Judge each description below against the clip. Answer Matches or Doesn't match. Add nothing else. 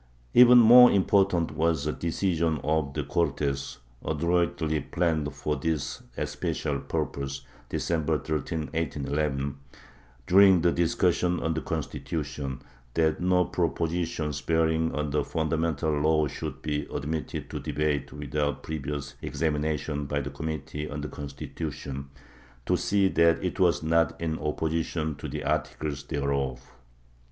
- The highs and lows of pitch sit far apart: Doesn't match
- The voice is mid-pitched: Doesn't match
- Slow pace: Matches